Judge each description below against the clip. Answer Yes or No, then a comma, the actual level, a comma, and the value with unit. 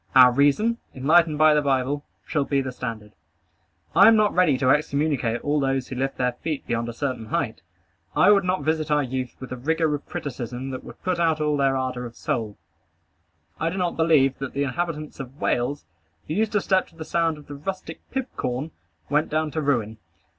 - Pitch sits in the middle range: Yes, medium, 145 Hz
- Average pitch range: Yes, average, 3.9 semitones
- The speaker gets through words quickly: Yes, fast, 210 wpm